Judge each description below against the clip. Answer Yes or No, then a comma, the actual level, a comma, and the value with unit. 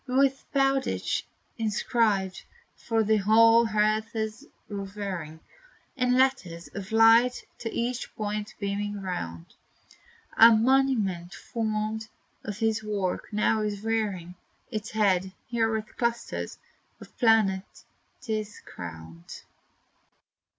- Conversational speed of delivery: No, slow, 105 wpm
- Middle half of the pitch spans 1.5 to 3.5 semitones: Yes, narrow, 2.5 semitones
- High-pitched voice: Yes, high, 215 Hz